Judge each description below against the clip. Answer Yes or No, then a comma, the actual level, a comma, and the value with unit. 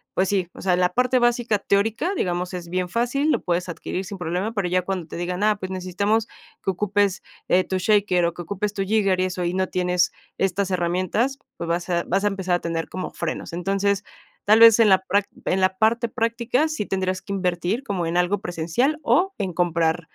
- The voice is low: No, high, 190 Hz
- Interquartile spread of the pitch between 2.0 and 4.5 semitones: Yes, average, 2.9 semitones